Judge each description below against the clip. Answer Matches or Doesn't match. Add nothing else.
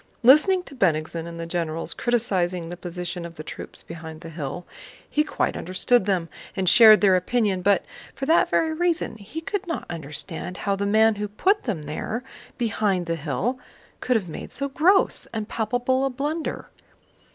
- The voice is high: Matches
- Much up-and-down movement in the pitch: Matches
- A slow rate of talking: Doesn't match